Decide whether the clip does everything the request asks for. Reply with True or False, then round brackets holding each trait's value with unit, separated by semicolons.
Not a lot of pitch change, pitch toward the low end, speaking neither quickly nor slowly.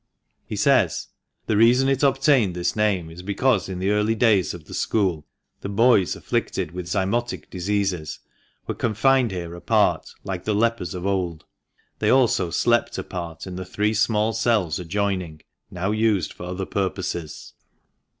False (3.9 semitones; 100 Hz; 160 wpm)